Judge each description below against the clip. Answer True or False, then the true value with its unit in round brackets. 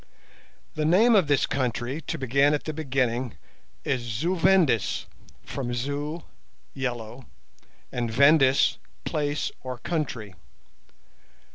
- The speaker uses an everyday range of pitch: True (4.0 semitones)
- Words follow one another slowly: True (110 wpm)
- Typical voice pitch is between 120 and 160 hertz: True (135 Hz)